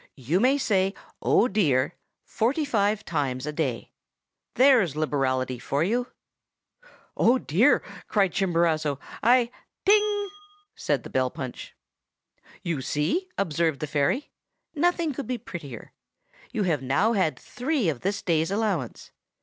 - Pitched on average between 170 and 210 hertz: Yes, medium, 185 Hz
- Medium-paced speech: No, slow, 130 wpm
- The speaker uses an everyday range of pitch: No, wide, 8.7 semitones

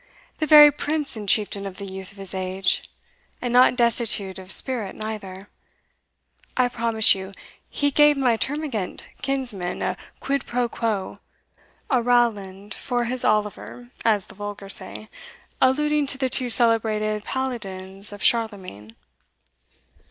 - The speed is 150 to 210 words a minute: No, slow, 135 wpm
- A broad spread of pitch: No, average, 4.4 semitones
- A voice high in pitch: Yes, high, 220 Hz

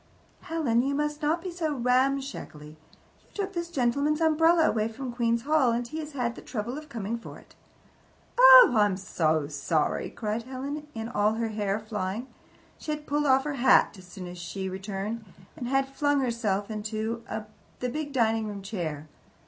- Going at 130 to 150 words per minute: No, average, 180 wpm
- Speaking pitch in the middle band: No, high, 235 Hz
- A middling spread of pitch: No, wide, 5.8 semitones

